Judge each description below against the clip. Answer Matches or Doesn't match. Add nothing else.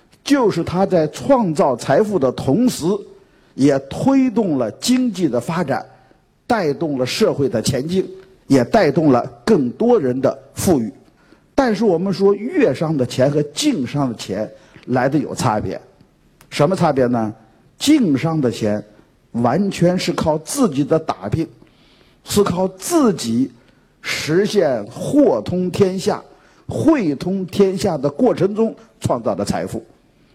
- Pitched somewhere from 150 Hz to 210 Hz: Matches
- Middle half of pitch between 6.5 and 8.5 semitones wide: Matches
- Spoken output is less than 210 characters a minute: Matches